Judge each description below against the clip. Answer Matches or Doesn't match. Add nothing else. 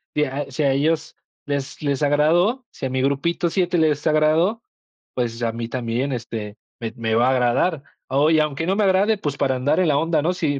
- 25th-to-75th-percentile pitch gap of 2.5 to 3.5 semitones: Doesn't match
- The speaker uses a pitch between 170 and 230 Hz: Doesn't match